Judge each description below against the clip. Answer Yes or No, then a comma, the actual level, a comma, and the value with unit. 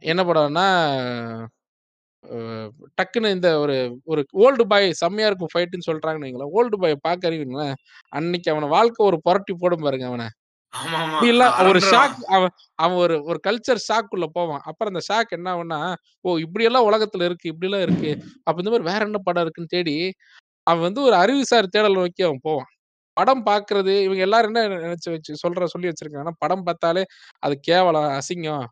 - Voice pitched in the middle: Yes, medium, 175 Hz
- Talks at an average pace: No, fast, 165 wpm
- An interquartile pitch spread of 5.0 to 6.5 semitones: No, average, 4.3 semitones